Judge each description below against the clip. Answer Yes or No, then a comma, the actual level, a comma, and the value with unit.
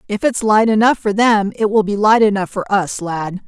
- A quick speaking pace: Yes, fast, 240 wpm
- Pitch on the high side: Yes, high, 205 Hz